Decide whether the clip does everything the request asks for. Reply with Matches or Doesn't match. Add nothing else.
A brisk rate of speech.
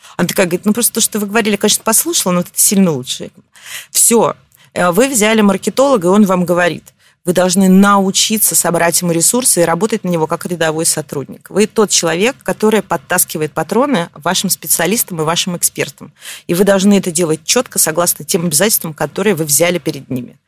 Matches